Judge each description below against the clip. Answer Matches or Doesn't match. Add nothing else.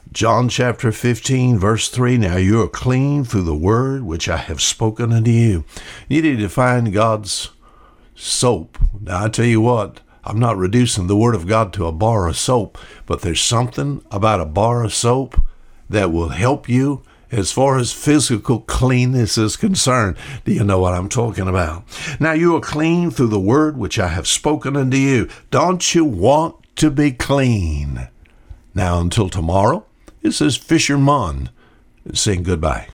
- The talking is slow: Doesn't match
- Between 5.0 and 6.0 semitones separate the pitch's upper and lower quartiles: Matches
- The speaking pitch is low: Matches